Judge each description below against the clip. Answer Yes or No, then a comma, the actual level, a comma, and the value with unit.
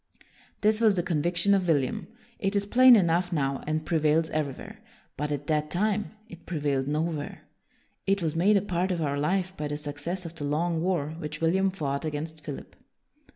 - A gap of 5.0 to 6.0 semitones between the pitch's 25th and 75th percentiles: No, average, 4.0 semitones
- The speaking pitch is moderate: Yes, medium, 165 Hz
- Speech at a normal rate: Yes, average, 185 wpm